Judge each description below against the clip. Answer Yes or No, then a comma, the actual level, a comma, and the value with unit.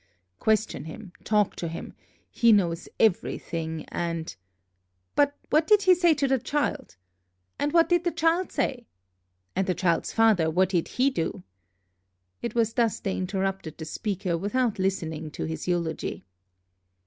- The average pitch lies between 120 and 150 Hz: No, high, 195 Hz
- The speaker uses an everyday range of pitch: No, wide, 7.5 semitones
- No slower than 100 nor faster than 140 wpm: No, average, 155 wpm